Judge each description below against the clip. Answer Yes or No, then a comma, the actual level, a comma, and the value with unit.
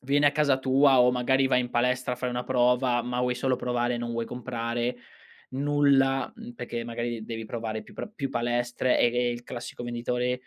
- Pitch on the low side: Yes, low, 125 Hz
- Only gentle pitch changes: Yes, narrow, 1.7 semitones